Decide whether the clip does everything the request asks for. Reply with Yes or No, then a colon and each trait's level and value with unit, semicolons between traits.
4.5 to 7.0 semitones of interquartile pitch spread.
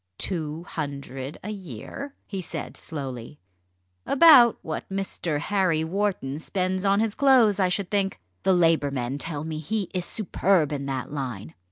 Yes: wide, 5.6 semitones